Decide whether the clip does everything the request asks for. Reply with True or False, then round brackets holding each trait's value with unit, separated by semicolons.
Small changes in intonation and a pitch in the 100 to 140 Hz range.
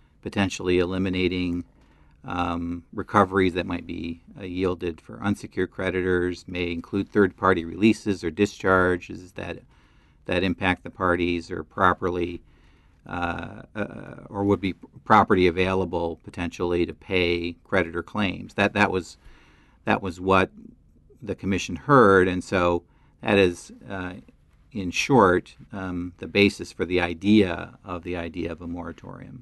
False (2.0 semitones; 90 Hz)